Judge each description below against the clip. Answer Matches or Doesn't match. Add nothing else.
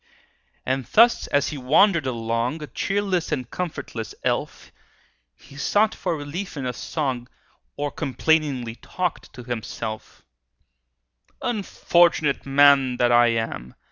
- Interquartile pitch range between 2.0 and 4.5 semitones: Doesn't match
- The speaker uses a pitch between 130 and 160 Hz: Matches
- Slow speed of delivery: Matches